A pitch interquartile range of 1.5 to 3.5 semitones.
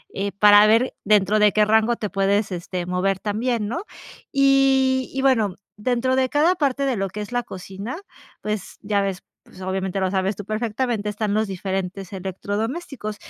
No: average, 4.0 semitones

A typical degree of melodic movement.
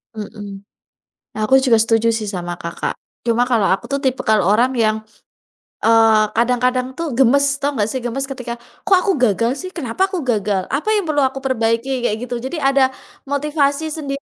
Yes: average, 3.8 semitones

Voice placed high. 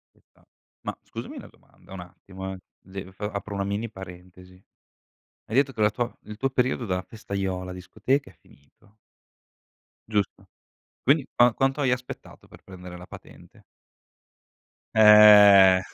No: low, 100 Hz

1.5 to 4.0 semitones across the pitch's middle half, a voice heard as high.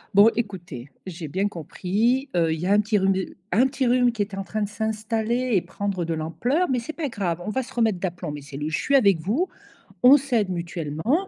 No: wide, 5.6 semitones; high, 205 Hz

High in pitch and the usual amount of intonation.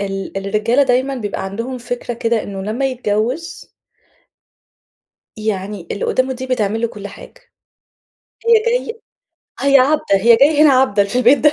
Yes: high, 235 Hz; average, 4.6 semitones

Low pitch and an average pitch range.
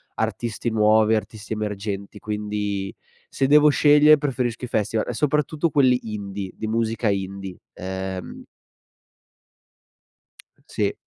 Yes: low, 110 Hz; average, 4.0 semitones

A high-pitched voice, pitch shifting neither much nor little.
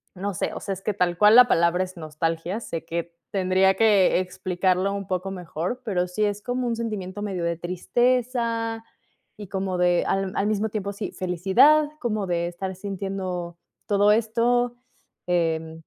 Yes: high, 195 Hz; average, 3.3 semitones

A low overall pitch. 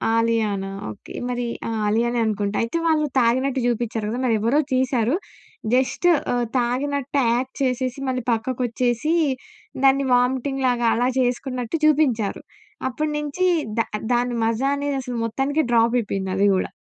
No: high, 245 Hz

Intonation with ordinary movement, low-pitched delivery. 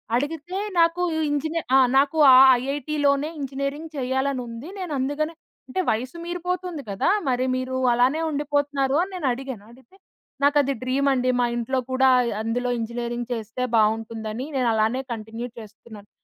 No: average, 3.4 semitones; very high, 265 Hz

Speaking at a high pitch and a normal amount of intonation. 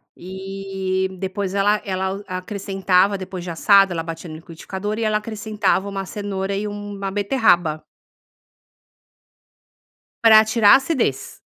No: high, 195 Hz; narrow, 1.7 semitones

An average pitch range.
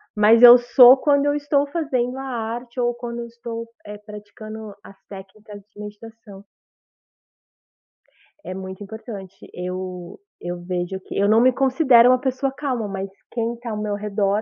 Yes: average, 3.5 semitones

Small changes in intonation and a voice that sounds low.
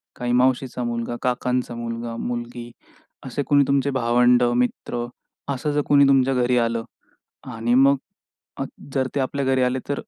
Yes: narrow, 1.9 semitones; low, 125 Hz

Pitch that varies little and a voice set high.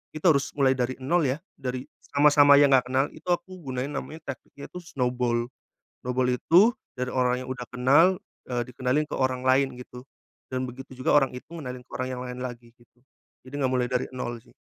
No: narrow, 2.2 semitones; low, 130 Hz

